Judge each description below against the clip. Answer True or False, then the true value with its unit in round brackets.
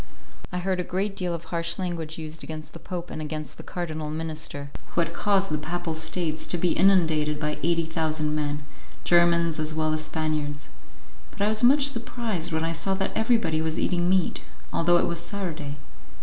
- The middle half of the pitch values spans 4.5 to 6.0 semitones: False (2.5 semitones)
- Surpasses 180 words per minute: True (190 wpm)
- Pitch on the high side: False (165 Hz)